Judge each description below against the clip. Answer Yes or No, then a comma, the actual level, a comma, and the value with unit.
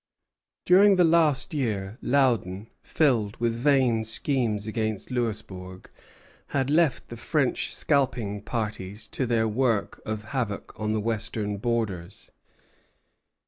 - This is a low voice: Yes, low, 115 Hz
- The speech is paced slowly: Yes, slow, 115 wpm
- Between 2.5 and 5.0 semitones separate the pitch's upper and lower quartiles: Yes, average, 4.1 semitones